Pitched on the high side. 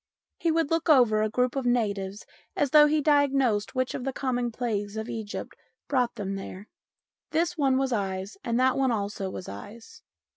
Yes: high, 245 Hz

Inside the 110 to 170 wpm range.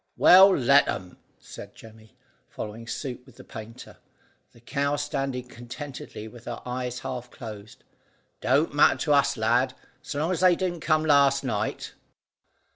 Yes: average, 150 wpm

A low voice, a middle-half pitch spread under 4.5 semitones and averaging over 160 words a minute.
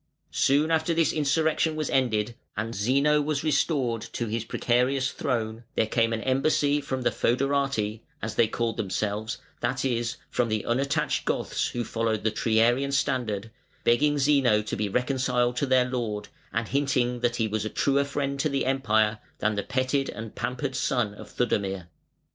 Yes: low, 125 Hz; average, 3.9 semitones; average, 170 wpm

